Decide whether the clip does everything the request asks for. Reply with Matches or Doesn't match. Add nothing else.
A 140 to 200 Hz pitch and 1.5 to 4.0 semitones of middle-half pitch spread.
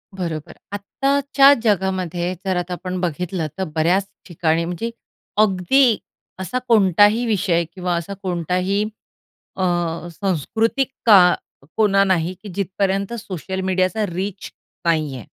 Matches